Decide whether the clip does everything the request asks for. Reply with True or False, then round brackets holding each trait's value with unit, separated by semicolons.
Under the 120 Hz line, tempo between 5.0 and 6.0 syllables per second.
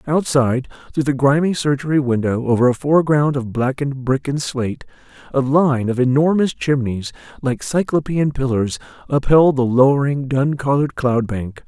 False (135 Hz; 5.1 syllables/s)